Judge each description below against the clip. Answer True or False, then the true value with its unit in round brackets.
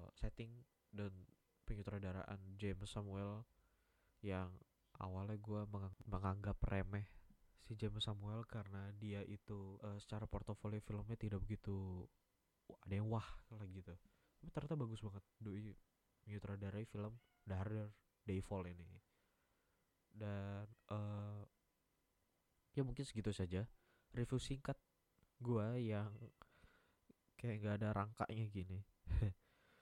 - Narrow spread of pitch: True (1.9 semitones)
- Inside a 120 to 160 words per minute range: False (105 wpm)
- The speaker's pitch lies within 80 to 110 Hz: True (105 Hz)